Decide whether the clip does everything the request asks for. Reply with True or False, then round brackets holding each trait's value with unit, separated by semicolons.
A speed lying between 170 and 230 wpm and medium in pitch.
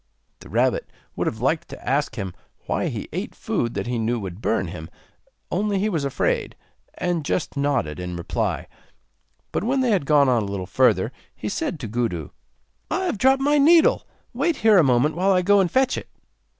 True (200 wpm; 145 Hz)